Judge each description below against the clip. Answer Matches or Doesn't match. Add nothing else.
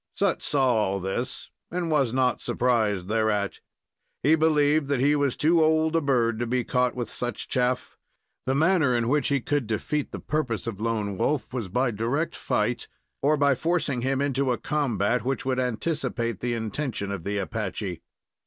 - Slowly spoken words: Doesn't match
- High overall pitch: Doesn't match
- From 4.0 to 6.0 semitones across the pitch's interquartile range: Matches